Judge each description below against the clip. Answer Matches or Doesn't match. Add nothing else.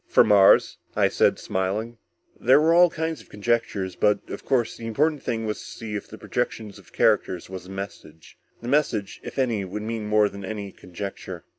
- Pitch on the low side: Matches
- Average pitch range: Matches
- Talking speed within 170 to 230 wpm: Matches